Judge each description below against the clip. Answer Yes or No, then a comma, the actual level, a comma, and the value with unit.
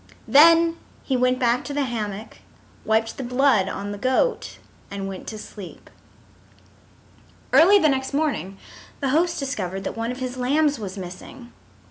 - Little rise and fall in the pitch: No, wide, 5.5 semitones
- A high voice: Yes, very high, 250 Hz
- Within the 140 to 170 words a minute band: Yes, average, 155 wpm